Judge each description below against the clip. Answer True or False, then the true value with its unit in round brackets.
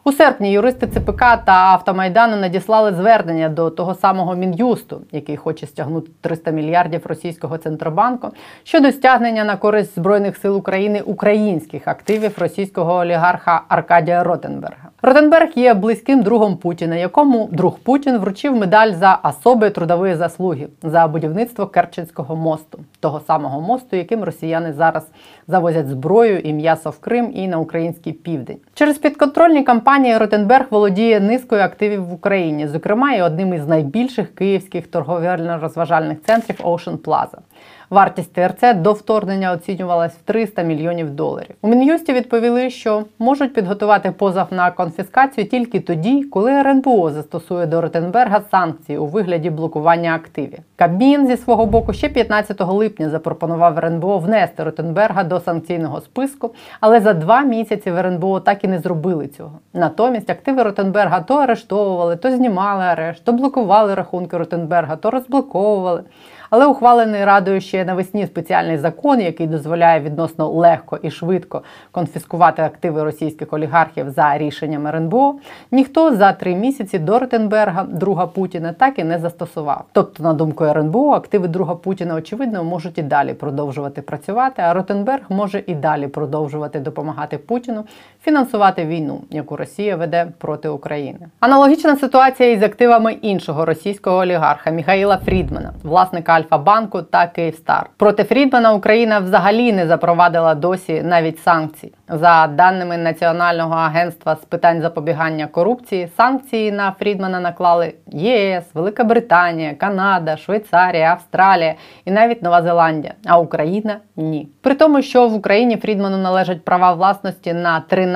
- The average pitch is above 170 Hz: True (185 Hz)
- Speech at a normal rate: True (140 wpm)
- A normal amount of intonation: True (4.6 semitones)